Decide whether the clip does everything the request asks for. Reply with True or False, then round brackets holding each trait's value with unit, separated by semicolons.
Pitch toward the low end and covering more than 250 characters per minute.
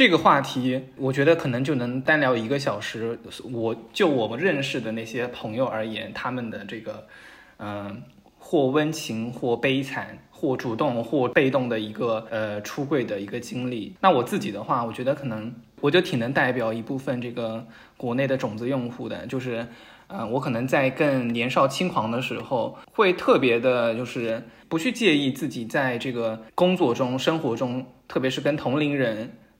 True (125 Hz; 270 characters per minute)